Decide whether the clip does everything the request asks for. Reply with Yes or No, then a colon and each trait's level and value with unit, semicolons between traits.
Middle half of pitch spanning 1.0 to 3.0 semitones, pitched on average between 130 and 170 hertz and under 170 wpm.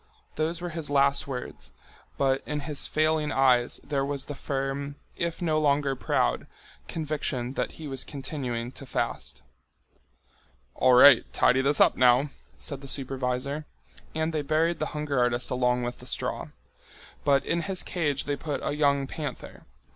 Yes: narrow, 2.6 semitones; medium, 140 Hz; average, 160 wpm